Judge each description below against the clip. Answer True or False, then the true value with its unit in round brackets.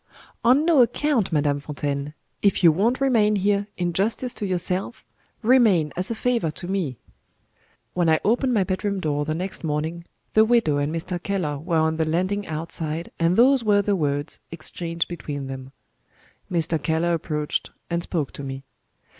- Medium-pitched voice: True (175 Hz)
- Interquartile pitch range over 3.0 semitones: True (4.9 semitones)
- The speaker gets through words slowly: False (170 wpm)